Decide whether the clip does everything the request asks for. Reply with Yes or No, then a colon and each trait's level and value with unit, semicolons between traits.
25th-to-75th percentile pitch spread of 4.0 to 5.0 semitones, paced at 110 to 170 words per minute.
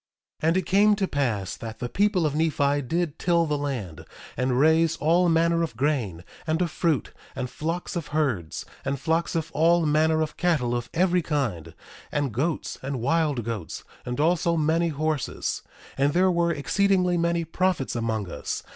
No: average, 4.4 semitones; average, 180 wpm